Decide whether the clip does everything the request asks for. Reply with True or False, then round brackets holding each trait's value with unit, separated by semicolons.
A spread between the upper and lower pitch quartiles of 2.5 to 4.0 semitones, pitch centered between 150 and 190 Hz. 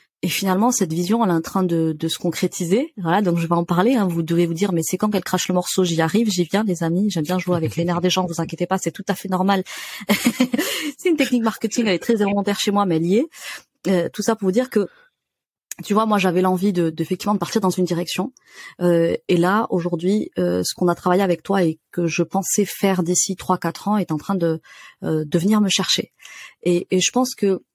True (3.0 semitones; 185 Hz)